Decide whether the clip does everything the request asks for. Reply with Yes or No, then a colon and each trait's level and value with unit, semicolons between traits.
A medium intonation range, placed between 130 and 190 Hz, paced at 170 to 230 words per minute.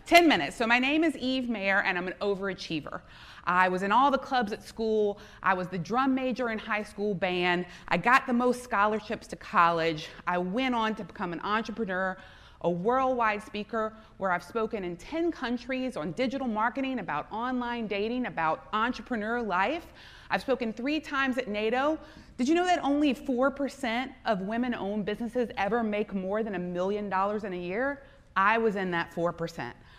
No: average, 5.0 semitones; high, 220 Hz; average, 185 wpm